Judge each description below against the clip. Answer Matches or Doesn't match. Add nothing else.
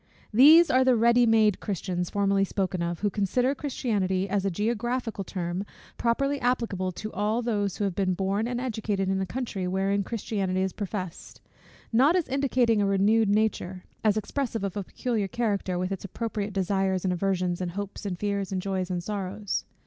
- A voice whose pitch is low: Doesn't match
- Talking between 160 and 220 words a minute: Matches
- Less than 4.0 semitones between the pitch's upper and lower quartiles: Matches